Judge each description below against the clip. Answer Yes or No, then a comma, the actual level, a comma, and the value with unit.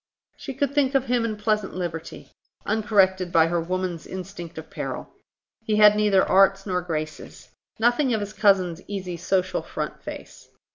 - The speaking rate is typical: Yes, average, 160 wpm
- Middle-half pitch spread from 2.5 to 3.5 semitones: Yes, average, 3.2 semitones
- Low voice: No, high, 195 Hz